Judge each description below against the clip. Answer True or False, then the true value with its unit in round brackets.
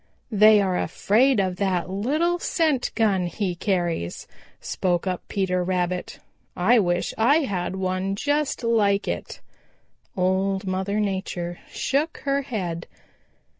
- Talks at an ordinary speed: False (125 wpm)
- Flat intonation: False (4.0 semitones)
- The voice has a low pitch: False (195 Hz)